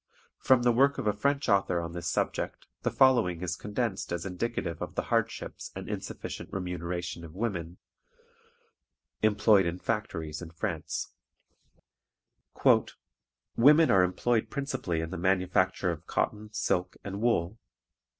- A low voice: Yes, very low, 95 Hz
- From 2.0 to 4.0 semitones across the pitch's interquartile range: No, average, 4.9 semitones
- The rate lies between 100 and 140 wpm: Yes, slow, 135 wpm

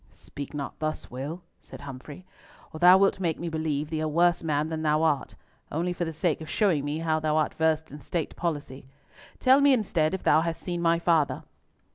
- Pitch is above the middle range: No, medium, 160 Hz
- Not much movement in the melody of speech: Yes, narrow, 2.3 semitones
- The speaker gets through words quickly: Yes, fast, 210 wpm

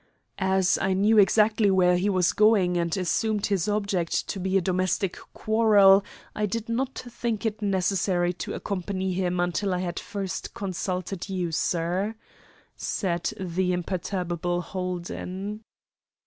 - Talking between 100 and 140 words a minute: Yes, slow, 135 wpm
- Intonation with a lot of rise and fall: No, narrow, 2.4 semitones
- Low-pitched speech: No, high, 190 Hz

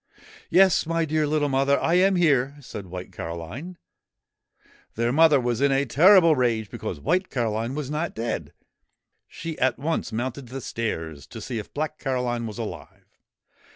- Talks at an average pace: Yes, average, 170 wpm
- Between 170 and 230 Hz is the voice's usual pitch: No, low, 135 Hz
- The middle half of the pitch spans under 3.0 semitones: No, average, 5.2 semitones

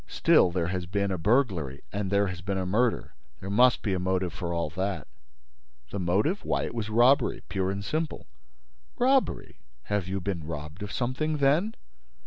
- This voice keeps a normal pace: Yes, average, 180 wpm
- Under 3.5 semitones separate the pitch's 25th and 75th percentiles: No, average, 5.0 semitones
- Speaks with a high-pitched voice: No, low, 100 Hz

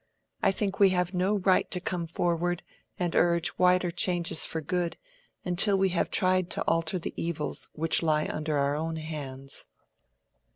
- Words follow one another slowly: No, average, 165 wpm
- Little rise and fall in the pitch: Yes, narrow, 2.2 semitones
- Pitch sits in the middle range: Yes, medium, 175 Hz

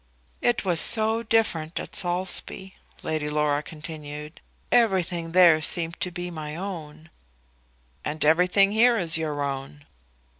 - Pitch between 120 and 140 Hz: No, medium, 165 Hz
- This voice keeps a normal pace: No, slow, 125 wpm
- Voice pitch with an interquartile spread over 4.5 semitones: No, average, 3.8 semitones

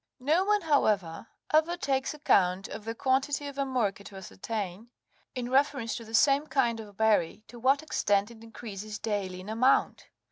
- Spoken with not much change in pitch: No, average, 5.0 semitones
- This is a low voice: No, high, 230 Hz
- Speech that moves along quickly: No, average, 170 wpm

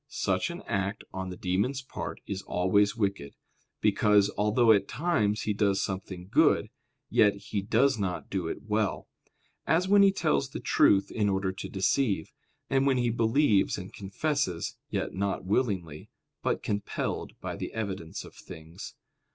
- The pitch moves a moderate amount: Yes, average, 3.1 semitones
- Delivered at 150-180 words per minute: Yes, average, 160 wpm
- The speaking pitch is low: Yes, low, 100 Hz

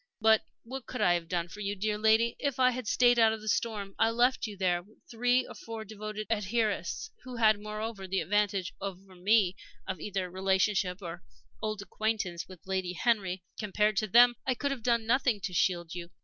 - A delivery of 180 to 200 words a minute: Yes, average, 195 wpm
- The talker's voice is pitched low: No, high, 210 Hz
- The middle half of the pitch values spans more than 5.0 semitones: No, average, 3.3 semitones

